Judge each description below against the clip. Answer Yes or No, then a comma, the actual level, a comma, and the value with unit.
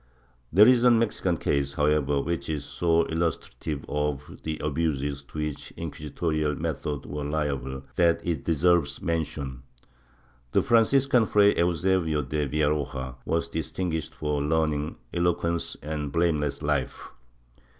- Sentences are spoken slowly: Yes, slow, 130 wpm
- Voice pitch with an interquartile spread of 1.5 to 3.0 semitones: Yes, narrow, 2.6 semitones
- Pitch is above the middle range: No, very low, 75 Hz